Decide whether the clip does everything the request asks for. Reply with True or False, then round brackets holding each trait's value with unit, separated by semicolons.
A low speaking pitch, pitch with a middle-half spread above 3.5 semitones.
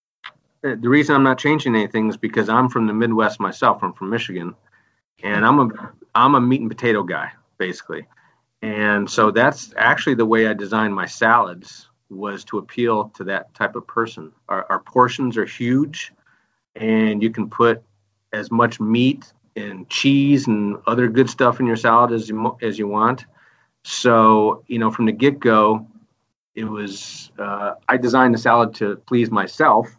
False (115 Hz; 2.4 semitones)